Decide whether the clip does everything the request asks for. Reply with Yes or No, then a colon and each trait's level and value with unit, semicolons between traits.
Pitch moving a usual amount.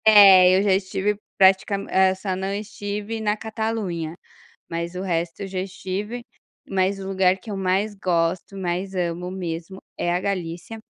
No: narrow, 2.0 semitones